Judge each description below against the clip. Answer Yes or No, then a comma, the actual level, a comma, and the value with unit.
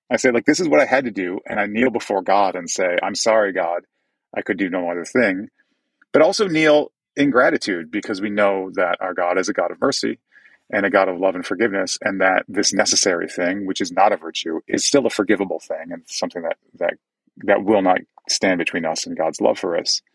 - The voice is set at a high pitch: No, low, 100 Hz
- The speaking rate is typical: No, fast, 235 wpm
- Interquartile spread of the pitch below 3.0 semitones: No, average, 3.3 semitones